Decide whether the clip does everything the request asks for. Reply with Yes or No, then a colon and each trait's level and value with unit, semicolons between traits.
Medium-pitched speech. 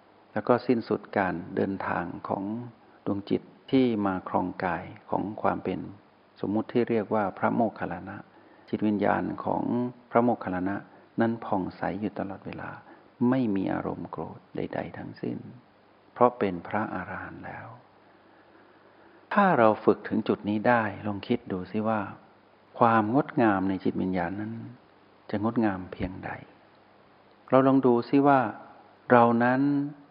No: low, 110 Hz